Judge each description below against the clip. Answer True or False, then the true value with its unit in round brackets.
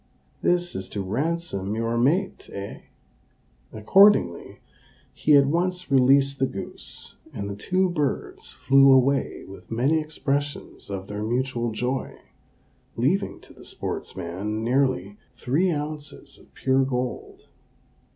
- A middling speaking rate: False (120 wpm)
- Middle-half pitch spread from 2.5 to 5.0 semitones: False (5.5 semitones)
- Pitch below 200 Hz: True (135 Hz)